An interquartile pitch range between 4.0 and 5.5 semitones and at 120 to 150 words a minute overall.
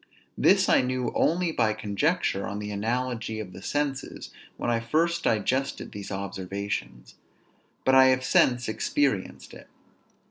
Yes: average, 4.6 semitones; average, 140 wpm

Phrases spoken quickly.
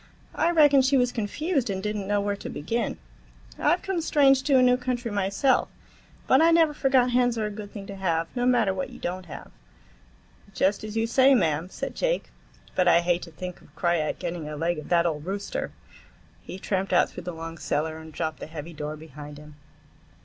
Yes: fast, 215 wpm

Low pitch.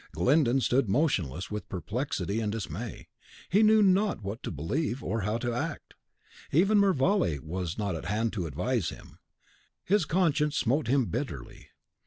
Yes: low, 120 Hz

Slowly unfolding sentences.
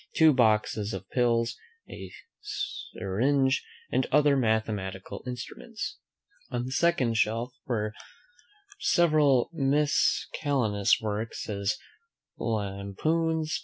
Yes: slow, 90 wpm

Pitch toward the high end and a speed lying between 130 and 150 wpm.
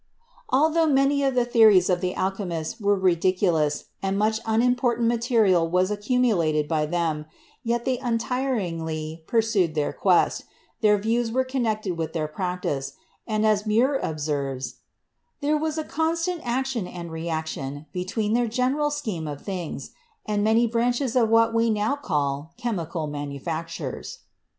Yes: high, 210 Hz; average, 145 wpm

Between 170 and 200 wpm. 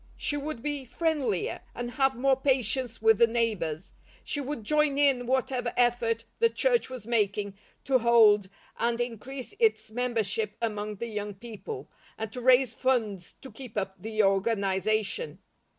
No: average, 150 wpm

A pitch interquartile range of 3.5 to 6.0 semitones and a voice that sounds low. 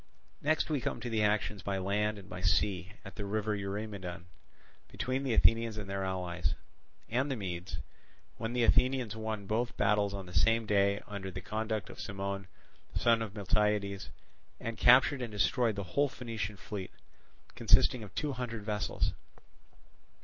No: average, 2.7 semitones; low, 105 Hz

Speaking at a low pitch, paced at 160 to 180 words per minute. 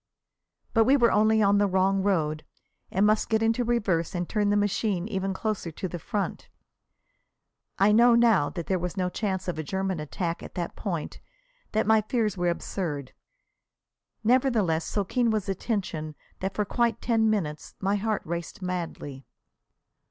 No: high, 195 Hz; average, 170 wpm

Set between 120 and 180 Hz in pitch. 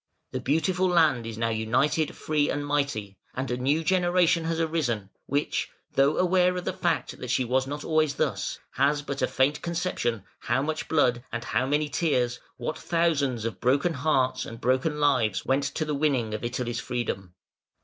Yes: medium, 140 Hz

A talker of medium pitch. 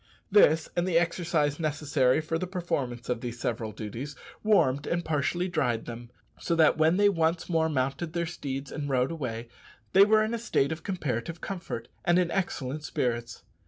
Yes: medium, 155 Hz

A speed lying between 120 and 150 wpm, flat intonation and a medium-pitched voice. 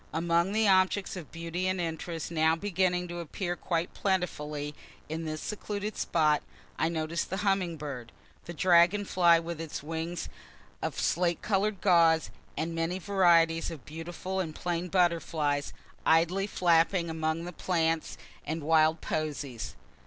Yes: average, 145 wpm; narrow, 2.2 semitones; medium, 170 Hz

